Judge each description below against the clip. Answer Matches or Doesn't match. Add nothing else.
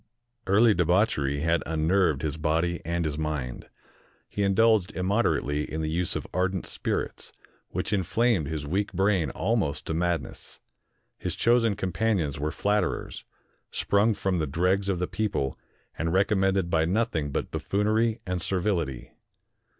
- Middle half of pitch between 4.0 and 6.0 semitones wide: Matches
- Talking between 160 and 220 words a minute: Doesn't match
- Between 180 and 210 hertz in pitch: Doesn't match